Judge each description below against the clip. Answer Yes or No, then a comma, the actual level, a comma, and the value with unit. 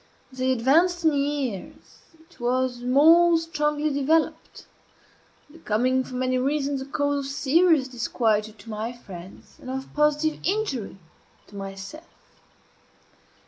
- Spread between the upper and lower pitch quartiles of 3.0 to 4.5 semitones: Yes, average, 3.8 semitones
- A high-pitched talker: Yes, very high, 270 Hz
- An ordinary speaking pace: No, slow, 125 wpm